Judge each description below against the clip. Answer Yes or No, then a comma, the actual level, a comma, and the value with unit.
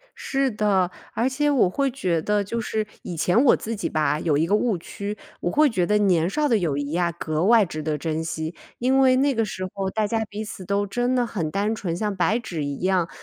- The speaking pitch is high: Yes, high, 200 Hz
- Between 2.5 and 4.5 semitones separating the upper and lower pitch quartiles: No, average, 5.2 semitones